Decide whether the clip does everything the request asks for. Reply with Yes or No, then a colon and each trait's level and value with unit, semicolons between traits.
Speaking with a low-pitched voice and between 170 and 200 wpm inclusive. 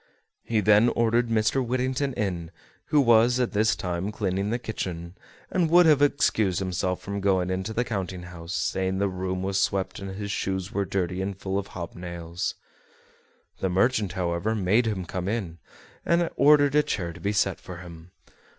Yes: low, 100 Hz; average, 180 wpm